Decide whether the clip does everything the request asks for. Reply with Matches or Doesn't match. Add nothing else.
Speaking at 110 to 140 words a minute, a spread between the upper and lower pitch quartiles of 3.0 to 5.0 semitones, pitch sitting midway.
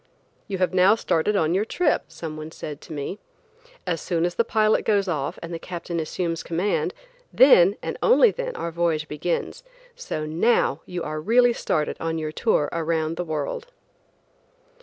Doesn't match